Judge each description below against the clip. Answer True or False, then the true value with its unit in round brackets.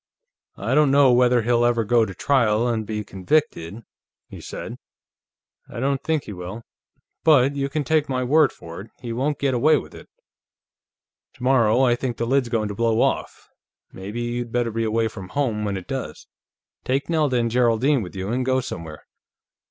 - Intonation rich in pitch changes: False (3.6 semitones)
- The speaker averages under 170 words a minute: False (185 wpm)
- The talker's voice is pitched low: True (120 Hz)